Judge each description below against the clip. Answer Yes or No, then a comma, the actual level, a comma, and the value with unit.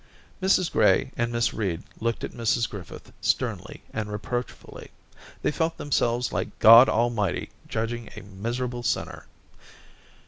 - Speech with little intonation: Yes, narrow, 2.2 semitones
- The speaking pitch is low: Yes, low, 115 Hz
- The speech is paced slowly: Yes, slow, 130 wpm